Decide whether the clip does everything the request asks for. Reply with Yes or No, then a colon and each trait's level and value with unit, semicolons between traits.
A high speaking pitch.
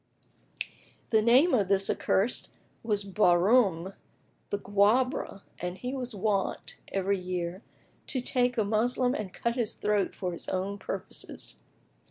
Yes: high, 205 Hz